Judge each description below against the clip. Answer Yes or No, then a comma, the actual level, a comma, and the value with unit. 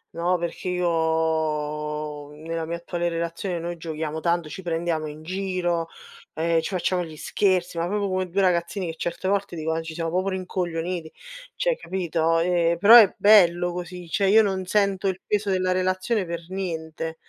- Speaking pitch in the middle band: Yes, medium, 175 Hz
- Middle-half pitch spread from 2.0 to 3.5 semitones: Yes, narrow, 2.4 semitones